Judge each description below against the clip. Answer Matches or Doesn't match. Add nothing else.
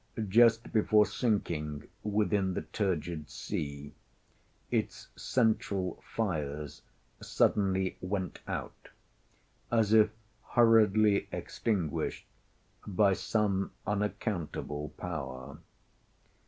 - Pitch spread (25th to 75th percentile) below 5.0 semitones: Doesn't match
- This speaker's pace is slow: Matches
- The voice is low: Matches